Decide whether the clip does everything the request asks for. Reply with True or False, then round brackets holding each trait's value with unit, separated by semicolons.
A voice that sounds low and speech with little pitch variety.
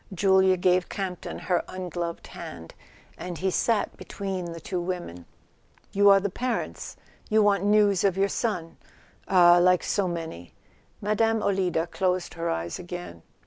False (185 Hz; 2.3 semitones)